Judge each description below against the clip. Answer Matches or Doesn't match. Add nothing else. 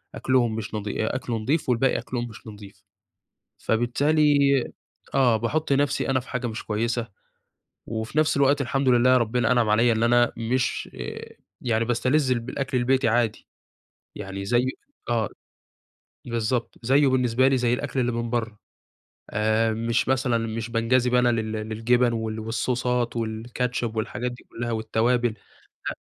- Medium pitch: Doesn't match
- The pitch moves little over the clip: Matches